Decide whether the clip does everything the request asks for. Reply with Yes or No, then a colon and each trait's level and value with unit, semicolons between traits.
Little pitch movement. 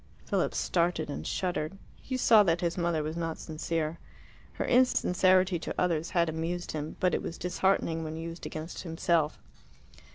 Yes: narrow, 2.0 semitones